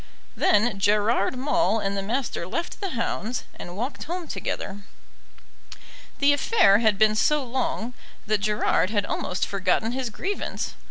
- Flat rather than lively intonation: No, average, 4.8 semitones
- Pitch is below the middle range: No, high, 220 Hz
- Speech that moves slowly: No, average, 145 wpm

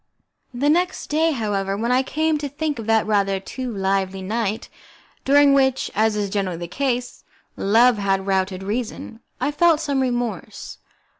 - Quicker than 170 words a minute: No, average, 160 wpm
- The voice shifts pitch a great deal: Yes, wide, 5.9 semitones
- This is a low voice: No, high, 230 Hz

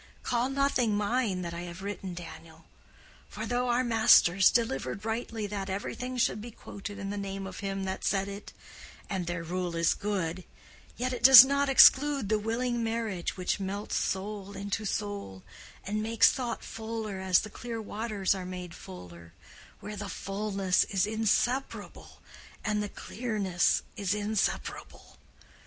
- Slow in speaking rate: No, average, 150 wpm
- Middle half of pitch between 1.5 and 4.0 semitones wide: Yes, average, 3.1 semitones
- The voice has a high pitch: Yes, high, 205 Hz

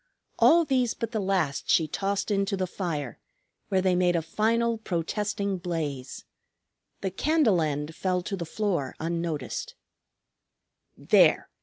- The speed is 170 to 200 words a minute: No, slow, 135 wpm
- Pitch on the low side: No, medium, 185 Hz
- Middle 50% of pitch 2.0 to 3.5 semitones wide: No, average, 4.2 semitones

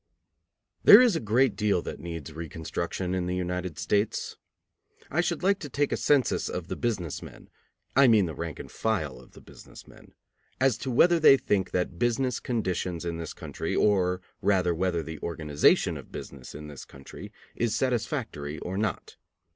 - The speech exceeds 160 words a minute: Yes, average, 180 wpm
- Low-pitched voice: Yes, very low, 95 Hz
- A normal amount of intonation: No, wide, 6.3 semitones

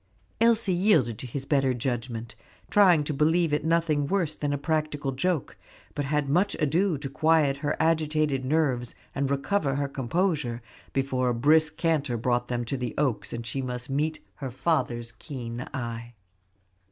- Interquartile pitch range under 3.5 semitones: No, average, 4.0 semitones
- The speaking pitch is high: No, medium, 140 Hz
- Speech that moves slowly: No, average, 165 wpm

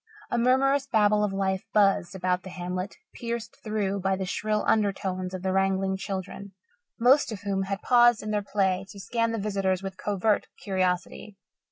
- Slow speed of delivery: No, average, 175 wpm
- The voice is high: Yes, high, 195 Hz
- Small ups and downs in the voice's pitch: Yes, narrow, 2.1 semitones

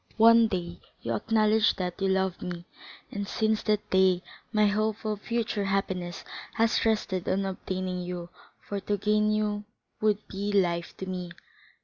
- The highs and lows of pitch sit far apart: No, narrow, 2.6 semitones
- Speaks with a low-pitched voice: No, high, 200 Hz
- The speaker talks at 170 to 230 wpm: No, average, 155 wpm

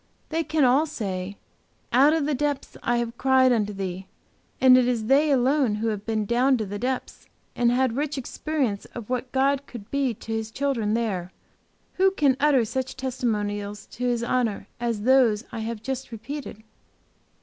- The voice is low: No, high, 245 Hz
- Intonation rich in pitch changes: No, average, 3.7 semitones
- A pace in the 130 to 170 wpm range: No, average, 180 wpm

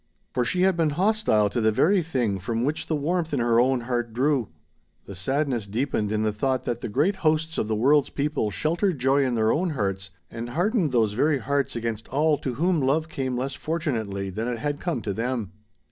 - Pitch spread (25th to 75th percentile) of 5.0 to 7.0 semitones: Yes, wide, 5.4 semitones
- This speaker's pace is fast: Yes, fast, 215 wpm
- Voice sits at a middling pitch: No, low, 130 Hz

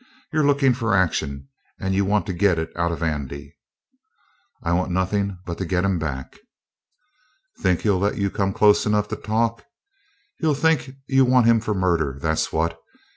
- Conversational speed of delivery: Yes, average, 180 wpm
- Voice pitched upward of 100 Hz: No, very low, 95 Hz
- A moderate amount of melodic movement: Yes, average, 4.8 semitones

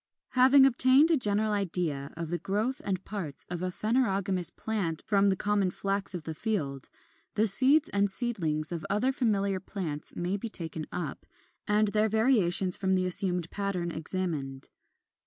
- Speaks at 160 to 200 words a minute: Yes, average, 165 wpm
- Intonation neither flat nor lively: Yes, average, 3.8 semitones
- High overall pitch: Yes, high, 195 Hz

